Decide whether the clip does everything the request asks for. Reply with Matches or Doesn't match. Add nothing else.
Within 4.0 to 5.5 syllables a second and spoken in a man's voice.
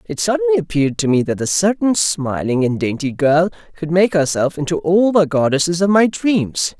Matches